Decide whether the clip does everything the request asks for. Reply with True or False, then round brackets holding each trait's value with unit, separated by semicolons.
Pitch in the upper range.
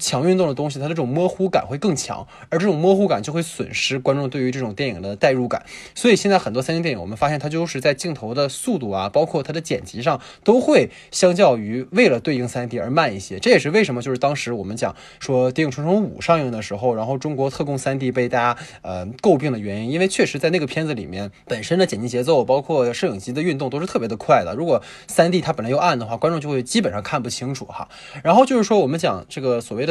False (140 Hz)